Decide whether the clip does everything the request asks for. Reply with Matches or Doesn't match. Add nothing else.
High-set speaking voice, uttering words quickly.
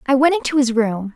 Matches